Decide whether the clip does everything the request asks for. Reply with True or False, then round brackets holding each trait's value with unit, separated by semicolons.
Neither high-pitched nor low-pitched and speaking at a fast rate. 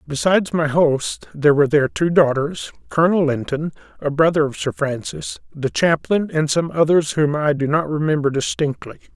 False (155 Hz; 170 wpm)